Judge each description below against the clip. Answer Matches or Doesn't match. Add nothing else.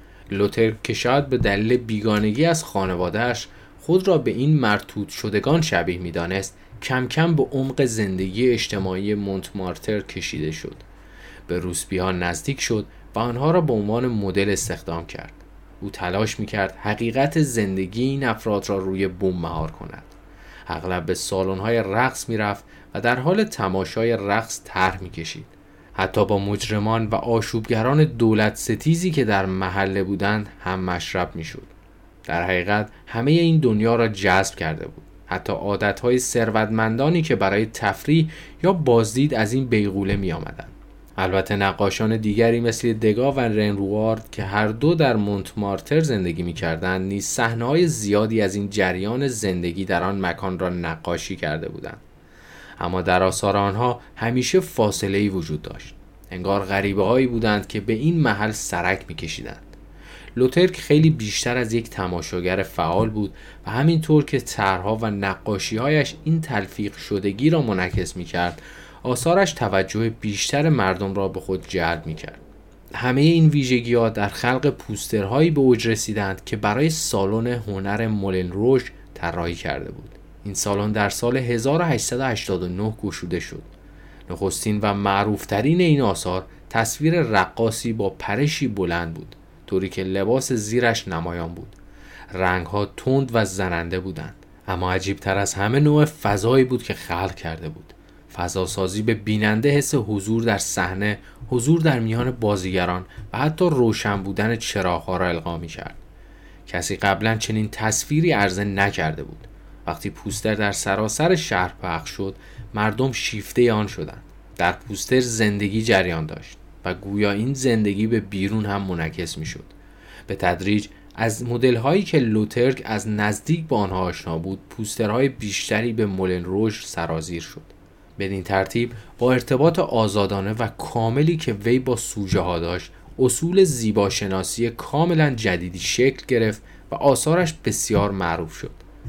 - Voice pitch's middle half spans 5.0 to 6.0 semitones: Doesn't match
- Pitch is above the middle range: Doesn't match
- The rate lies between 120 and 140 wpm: Doesn't match